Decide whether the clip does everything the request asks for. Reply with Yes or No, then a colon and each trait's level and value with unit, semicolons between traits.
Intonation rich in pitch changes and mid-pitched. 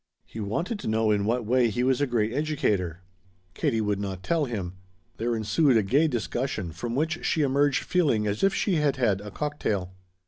No: wide, 5.8 semitones; low, 120 Hz